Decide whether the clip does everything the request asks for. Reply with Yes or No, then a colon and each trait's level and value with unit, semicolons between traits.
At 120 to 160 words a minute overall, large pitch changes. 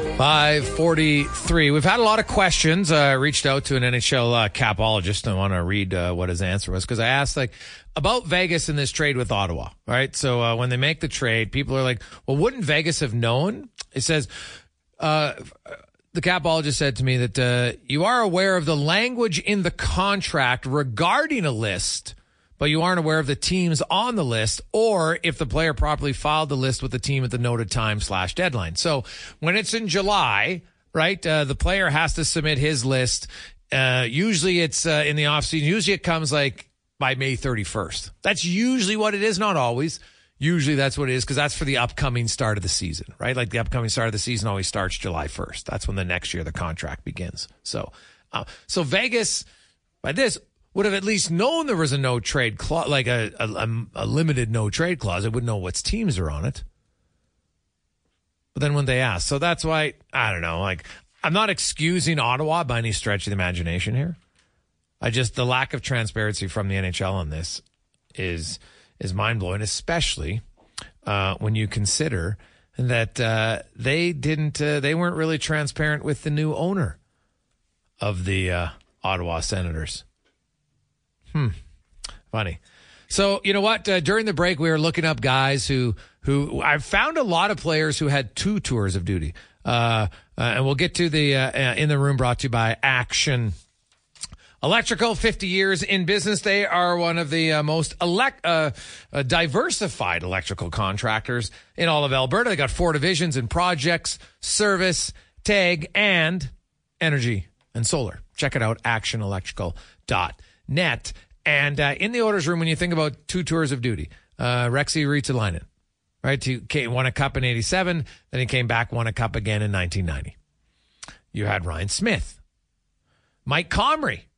No: average, 190 wpm; wide, 7.3 semitones